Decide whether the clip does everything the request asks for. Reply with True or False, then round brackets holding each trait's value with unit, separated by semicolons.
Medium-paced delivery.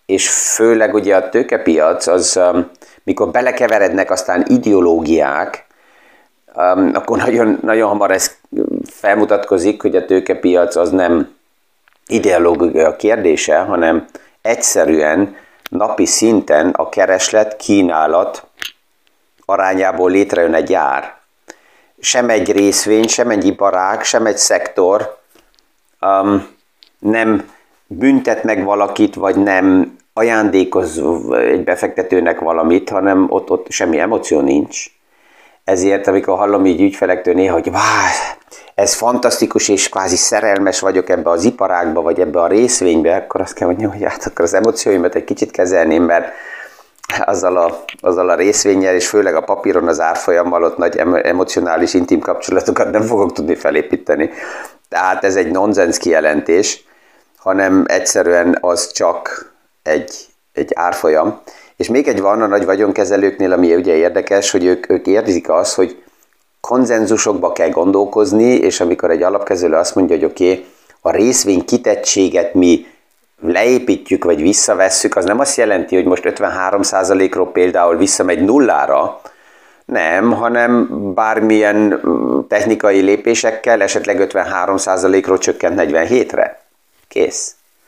True (125 wpm)